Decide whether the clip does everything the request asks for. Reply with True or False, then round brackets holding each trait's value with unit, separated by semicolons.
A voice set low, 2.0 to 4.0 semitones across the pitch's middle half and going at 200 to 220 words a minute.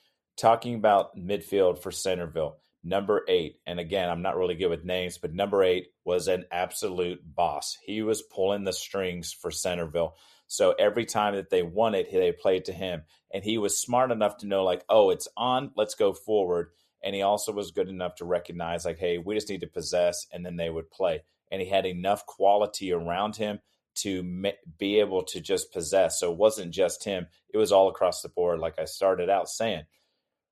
False (100 Hz; 4.9 semitones; 205 wpm)